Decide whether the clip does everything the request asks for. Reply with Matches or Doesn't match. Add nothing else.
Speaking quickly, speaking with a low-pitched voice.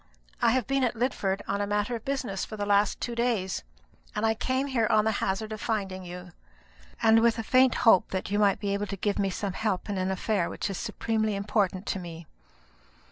Doesn't match